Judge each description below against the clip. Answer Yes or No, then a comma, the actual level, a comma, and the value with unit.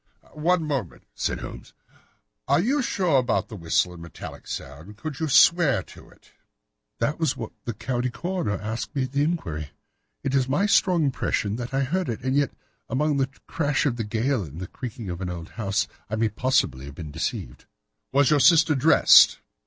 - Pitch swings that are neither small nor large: No, wide, 6.7 semitones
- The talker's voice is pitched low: Yes, low, 130 Hz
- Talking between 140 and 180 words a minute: No, average, 190 wpm